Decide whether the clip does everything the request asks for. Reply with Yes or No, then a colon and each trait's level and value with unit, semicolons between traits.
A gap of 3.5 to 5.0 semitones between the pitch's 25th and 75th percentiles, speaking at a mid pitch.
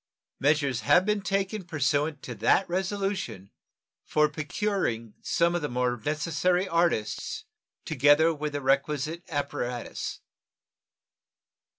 Yes: average, 4.5 semitones; medium, 150 Hz